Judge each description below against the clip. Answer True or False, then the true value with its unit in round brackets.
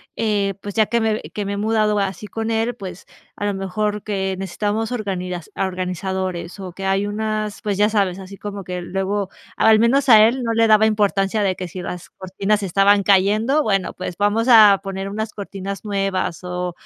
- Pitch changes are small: True (2.1 semitones)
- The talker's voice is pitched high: True (200 Hz)